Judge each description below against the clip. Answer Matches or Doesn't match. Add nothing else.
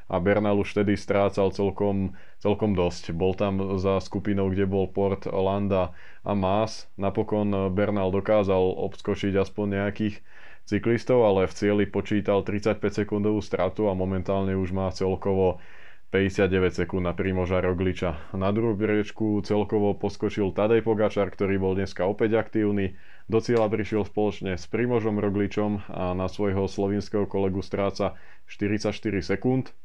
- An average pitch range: Doesn't match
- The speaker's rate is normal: Matches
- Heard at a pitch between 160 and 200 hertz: Doesn't match